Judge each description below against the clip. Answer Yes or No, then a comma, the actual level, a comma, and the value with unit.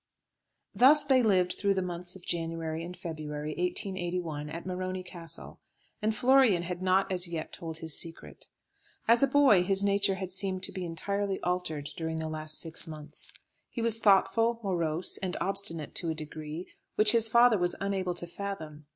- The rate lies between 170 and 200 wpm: Yes, average, 175 wpm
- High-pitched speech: No, medium, 180 Hz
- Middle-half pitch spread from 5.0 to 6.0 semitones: No, average, 3.4 semitones